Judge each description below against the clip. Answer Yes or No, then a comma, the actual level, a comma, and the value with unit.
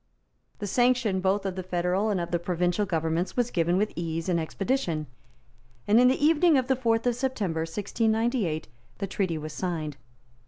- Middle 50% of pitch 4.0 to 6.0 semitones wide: Yes, wide, 5.4 semitones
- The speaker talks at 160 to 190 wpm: Yes, average, 180 wpm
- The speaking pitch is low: No, high, 190 Hz